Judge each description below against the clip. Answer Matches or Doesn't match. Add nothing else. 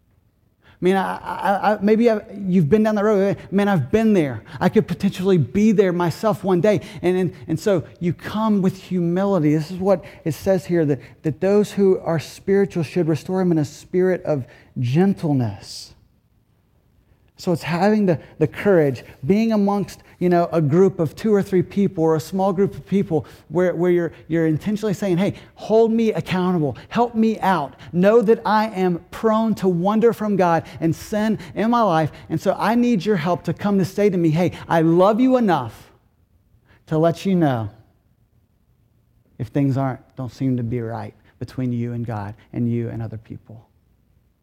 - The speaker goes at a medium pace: Matches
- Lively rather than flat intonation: Matches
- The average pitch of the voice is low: Doesn't match